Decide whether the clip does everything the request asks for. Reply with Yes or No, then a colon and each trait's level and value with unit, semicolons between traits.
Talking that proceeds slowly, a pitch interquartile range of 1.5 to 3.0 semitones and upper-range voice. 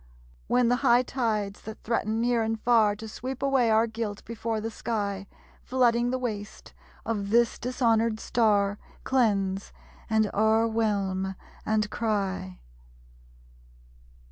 Yes: slow, 120 wpm; narrow, 2.4 semitones; high, 220 Hz